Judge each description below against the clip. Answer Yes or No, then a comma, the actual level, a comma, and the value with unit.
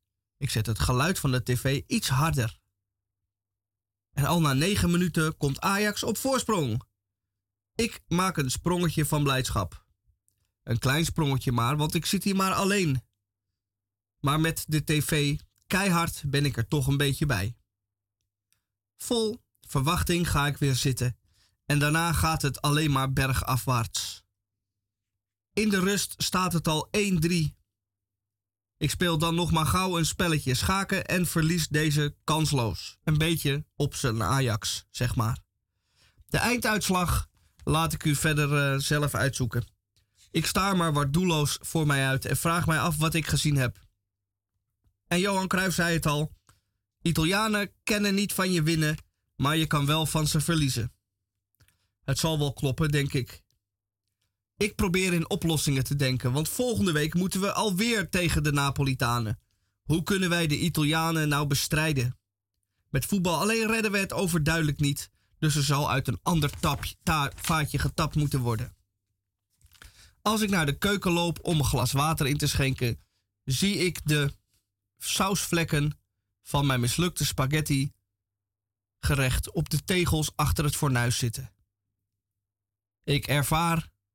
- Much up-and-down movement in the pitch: Yes, wide, 8.0 semitones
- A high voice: No, medium, 140 Hz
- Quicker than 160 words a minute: No, average, 150 wpm